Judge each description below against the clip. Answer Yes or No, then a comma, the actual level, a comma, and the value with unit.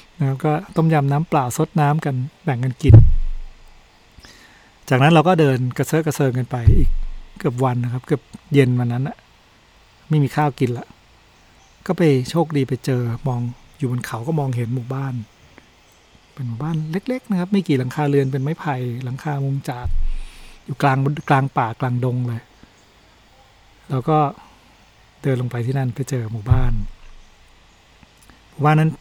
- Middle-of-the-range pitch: No, low, 130 Hz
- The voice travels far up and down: No, average, 4.1 semitones